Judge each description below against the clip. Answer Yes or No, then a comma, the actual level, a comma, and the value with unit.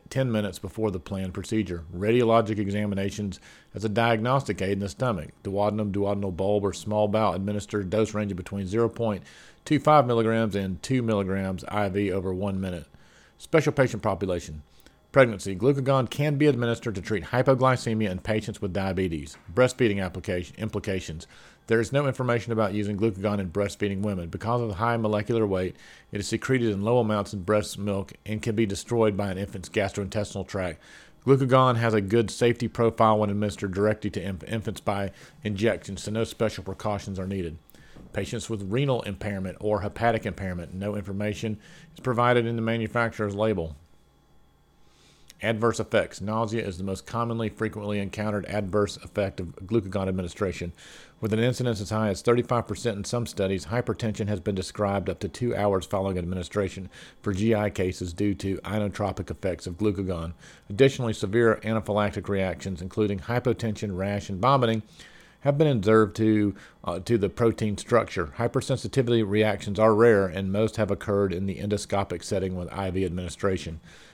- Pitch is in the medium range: No, low, 105 Hz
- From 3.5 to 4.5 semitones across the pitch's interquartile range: No, average, 2.8 semitones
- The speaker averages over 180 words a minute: No, average, 160 wpm